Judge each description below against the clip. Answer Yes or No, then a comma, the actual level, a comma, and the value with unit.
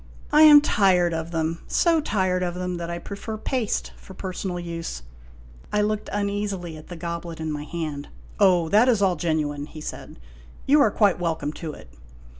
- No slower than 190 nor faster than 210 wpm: Yes, average, 195 wpm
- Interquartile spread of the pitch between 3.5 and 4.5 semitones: Yes, average, 4.0 semitones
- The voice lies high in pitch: No, medium, 175 Hz